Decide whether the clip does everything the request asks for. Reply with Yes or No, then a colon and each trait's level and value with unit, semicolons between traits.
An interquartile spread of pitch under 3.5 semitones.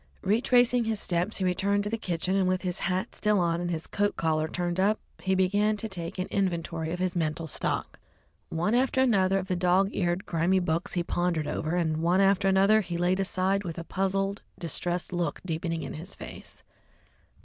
Yes: narrow, 2.5 semitones